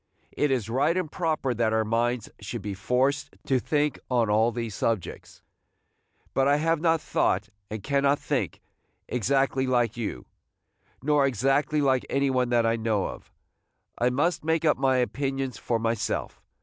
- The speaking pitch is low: Yes, low, 130 Hz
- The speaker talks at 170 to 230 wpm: No, average, 160 wpm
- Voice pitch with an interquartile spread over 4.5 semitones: No, average, 3.7 semitones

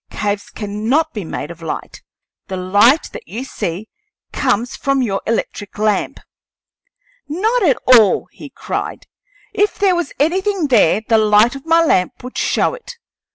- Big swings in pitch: Yes, wide, 7.7 semitones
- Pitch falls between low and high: No, high, 240 Hz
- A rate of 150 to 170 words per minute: Yes, average, 155 wpm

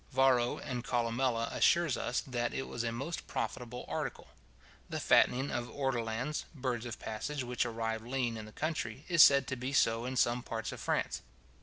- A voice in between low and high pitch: No, low, 120 Hz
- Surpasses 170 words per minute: Yes, average, 180 wpm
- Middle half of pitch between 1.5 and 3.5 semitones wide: Yes, narrow, 2.5 semitones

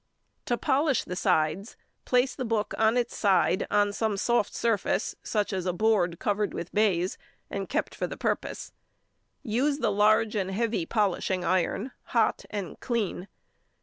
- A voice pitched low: No, high, 210 Hz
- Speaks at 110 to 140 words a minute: No, average, 160 wpm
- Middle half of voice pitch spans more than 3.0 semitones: Yes, average, 3.5 semitones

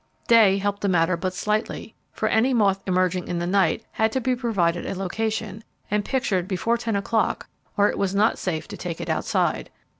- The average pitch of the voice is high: Yes, high, 200 Hz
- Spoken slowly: No, average, 200 wpm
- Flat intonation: No, average, 3.3 semitones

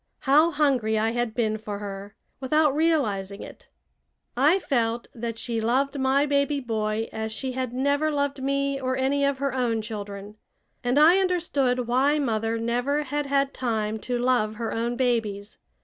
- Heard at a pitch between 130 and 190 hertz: No, very high, 250 Hz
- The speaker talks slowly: No, average, 165 wpm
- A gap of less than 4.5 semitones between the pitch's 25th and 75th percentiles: Yes, average, 4.0 semitones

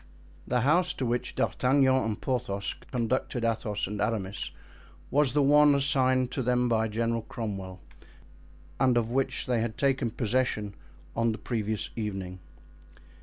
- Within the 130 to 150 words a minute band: Yes, average, 140 wpm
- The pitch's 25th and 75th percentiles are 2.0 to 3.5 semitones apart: Yes, average, 3.1 semitones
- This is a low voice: Yes, low, 120 Hz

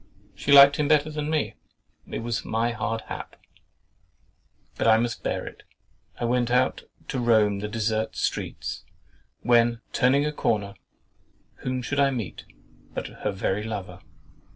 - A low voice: Yes, low, 120 Hz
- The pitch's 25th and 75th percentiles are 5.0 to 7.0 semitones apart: No, average, 3.9 semitones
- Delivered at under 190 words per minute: Yes, average, 145 wpm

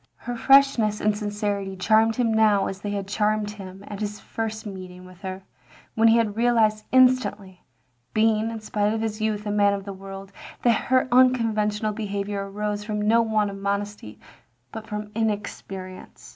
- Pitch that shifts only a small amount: Yes, narrow, 1.8 semitones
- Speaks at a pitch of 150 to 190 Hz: No, high, 210 Hz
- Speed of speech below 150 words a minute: No, average, 170 wpm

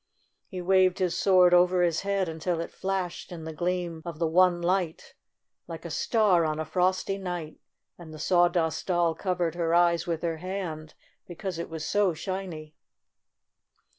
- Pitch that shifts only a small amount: Yes, narrow, 2.2 semitones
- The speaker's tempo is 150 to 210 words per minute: Yes, average, 165 wpm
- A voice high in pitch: No, medium, 175 Hz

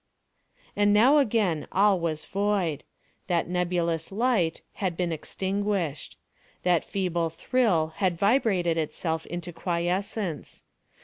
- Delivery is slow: Yes, slow, 110 wpm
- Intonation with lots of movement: No, average, 3.5 semitones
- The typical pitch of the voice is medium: Yes, medium, 180 Hz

